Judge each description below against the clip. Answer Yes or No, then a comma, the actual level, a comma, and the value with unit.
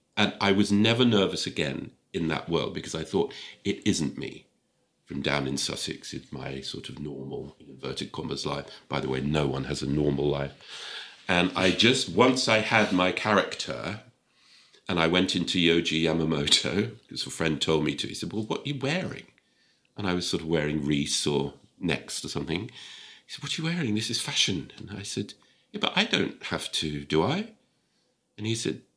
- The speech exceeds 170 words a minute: Yes, average, 200 wpm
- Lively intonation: Yes, wide, 7.1 semitones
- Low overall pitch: Yes, very low, 90 Hz